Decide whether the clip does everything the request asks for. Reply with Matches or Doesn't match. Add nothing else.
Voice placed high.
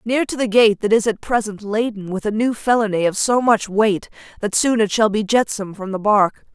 Matches